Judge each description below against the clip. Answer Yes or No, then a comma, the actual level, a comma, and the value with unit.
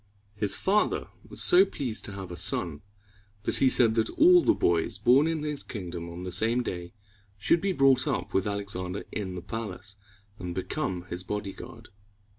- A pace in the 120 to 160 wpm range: No, average, 180 wpm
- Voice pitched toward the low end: Yes, low, 105 Hz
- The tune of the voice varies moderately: No, wide, 6.7 semitones